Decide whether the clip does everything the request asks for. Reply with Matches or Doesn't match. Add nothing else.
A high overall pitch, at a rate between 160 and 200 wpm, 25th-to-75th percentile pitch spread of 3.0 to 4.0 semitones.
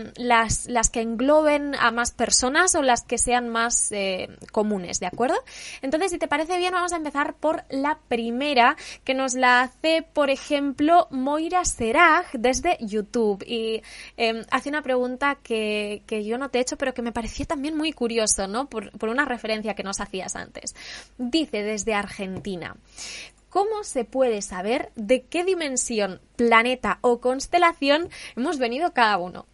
Doesn't match